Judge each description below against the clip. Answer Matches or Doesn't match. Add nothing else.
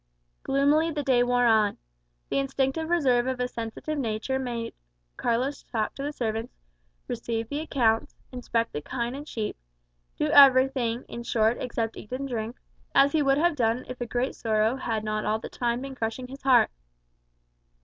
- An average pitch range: Matches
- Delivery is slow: Doesn't match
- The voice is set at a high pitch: Matches